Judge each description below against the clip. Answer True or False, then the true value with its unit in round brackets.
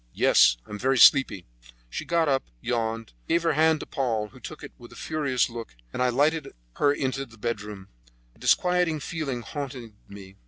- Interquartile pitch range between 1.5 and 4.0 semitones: False (4.9 semitones)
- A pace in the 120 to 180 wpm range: False (190 wpm)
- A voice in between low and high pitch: False (130 Hz)